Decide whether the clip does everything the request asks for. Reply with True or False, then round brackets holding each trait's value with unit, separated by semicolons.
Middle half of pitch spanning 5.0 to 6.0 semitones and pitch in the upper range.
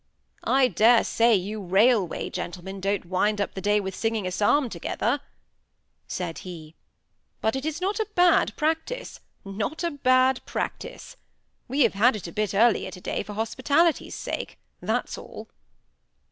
True (5.5 semitones; 220 Hz)